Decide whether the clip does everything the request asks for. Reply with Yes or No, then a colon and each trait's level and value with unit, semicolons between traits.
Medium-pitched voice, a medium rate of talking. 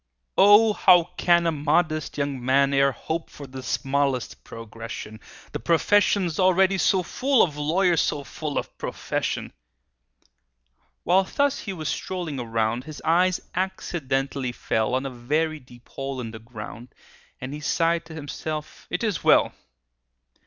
Yes: medium, 150 Hz; average, 145 wpm